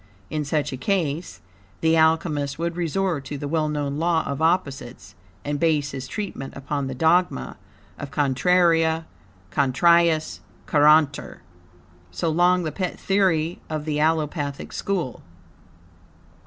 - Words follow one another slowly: Yes, slow, 130 wpm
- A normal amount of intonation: Yes, average, 3.0 semitones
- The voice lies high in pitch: No, medium, 155 Hz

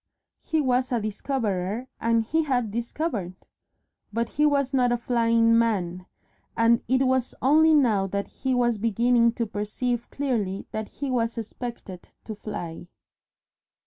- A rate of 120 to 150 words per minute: Yes, average, 145 wpm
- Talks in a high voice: Yes, high, 235 Hz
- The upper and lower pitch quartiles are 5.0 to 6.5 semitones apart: No, average, 3.3 semitones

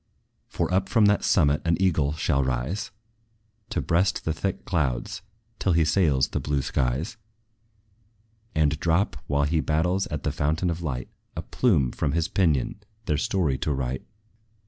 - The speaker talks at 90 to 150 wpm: No, average, 160 wpm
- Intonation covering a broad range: No, average, 4.4 semitones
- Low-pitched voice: Yes, very low, 80 Hz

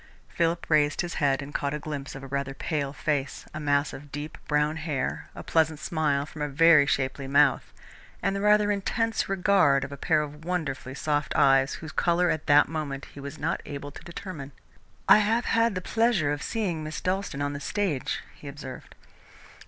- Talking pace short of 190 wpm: No, average, 195 wpm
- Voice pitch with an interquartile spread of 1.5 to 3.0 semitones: No, average, 3.4 semitones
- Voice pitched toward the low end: No, medium, 150 Hz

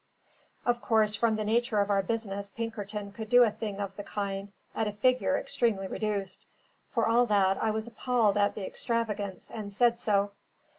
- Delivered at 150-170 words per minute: No, average, 185 wpm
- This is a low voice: No, high, 215 Hz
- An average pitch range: No, narrow, 2.3 semitones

